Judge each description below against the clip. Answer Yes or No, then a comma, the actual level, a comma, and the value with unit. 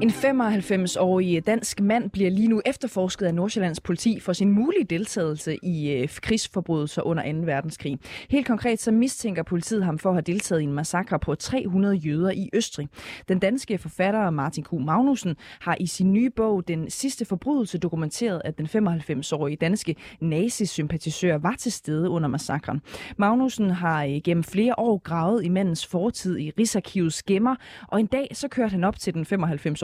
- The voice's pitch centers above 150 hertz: Yes, medium, 185 Hz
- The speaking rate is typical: Yes, average, 170 wpm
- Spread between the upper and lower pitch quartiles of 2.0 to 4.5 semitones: No, average, 5.2 semitones